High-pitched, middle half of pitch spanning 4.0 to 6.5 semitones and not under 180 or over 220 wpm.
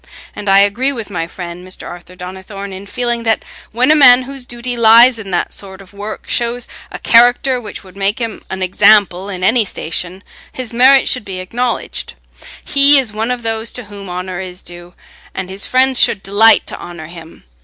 Yes: high, 205 Hz; average, 4.6 semitones; average, 195 wpm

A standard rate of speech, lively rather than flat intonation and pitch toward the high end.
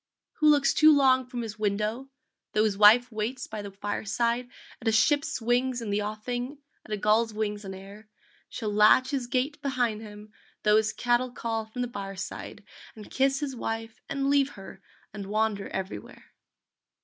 No: average, 180 wpm; average, 3.3 semitones; high, 225 Hz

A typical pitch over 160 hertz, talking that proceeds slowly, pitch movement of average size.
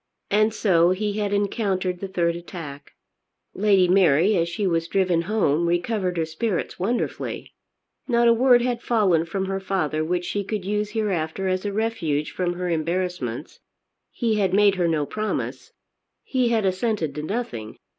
No: medium, 185 Hz; average, 165 wpm; average, 3.9 semitones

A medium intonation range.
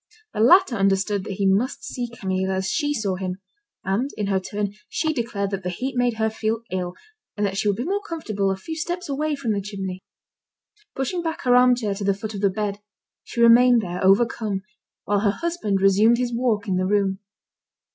Yes: average, 4.1 semitones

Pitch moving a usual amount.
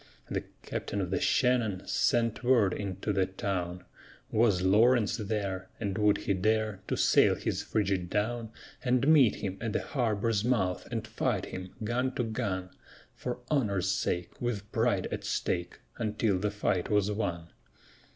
Yes: average, 3.6 semitones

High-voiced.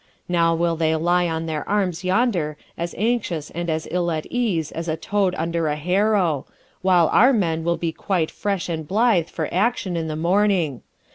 No: medium, 170 Hz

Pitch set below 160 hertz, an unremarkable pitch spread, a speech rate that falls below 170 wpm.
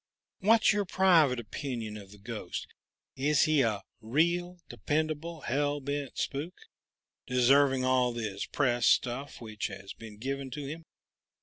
Yes: low, 135 Hz; average, 4.4 semitones; slow, 135 wpm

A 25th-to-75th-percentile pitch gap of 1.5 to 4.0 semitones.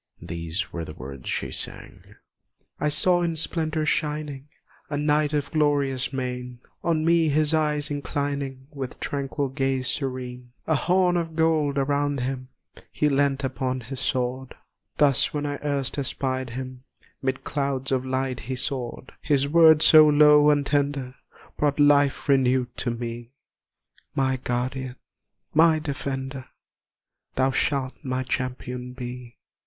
Yes: narrow, 2.4 semitones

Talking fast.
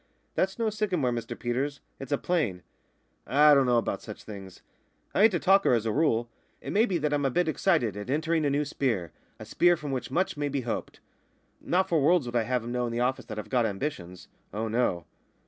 Yes: fast, 235 wpm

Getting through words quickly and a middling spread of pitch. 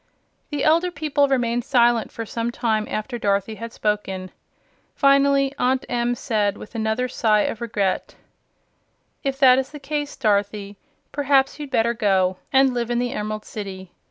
No: average, 155 wpm; average, 4.2 semitones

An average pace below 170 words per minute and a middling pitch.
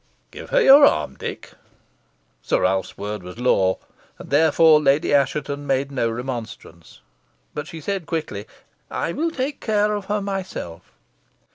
Yes: average, 145 wpm; medium, 145 Hz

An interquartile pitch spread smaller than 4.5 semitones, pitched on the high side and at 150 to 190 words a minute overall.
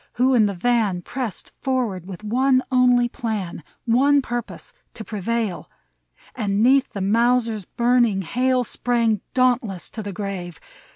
No: average, 3.9 semitones; high, 230 Hz; average, 140 wpm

